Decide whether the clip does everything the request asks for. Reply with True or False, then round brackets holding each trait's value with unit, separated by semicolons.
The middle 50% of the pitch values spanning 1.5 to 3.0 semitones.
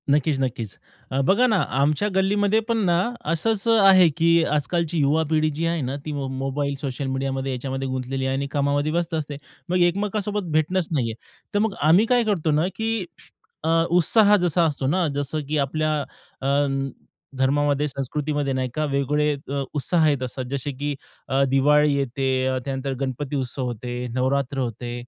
False (4.0 semitones)